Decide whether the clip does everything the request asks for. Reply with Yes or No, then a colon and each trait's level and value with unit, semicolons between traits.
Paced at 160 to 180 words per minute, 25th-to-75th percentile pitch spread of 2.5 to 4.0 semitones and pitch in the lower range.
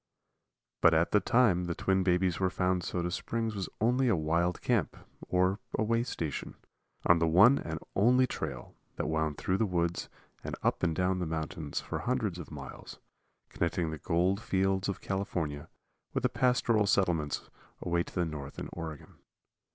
Yes: average, 165 wpm; average, 3.5 semitones; very low, 90 Hz